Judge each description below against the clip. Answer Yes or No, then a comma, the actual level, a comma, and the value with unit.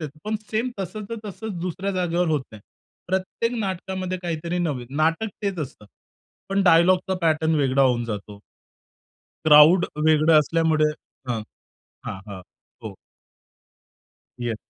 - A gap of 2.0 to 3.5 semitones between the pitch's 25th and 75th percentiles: No, average, 4.0 semitones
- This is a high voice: No, medium, 165 Hz